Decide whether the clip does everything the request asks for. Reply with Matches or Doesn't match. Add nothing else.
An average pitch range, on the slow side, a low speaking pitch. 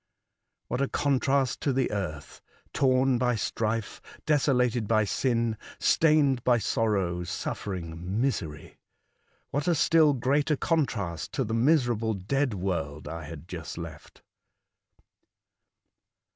Doesn't match